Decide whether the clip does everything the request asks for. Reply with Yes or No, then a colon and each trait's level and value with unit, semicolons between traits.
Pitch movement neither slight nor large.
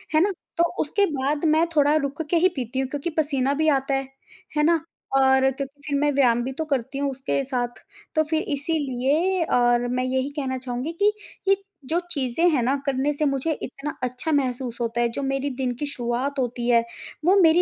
Yes: average, 3.1 semitones